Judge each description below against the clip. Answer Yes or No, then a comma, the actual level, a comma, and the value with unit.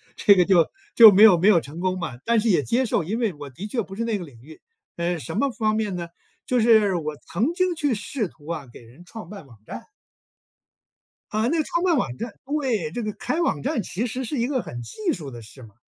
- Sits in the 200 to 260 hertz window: Yes, high, 205 Hz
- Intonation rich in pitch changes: Yes, wide, 6.5 semitones